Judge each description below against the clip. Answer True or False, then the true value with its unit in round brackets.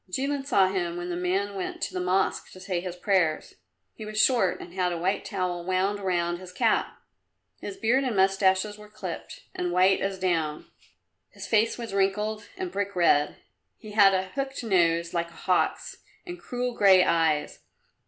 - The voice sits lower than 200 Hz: True (190 Hz)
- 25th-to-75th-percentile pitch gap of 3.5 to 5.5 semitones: False (2.9 semitones)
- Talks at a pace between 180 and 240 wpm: True (185 wpm)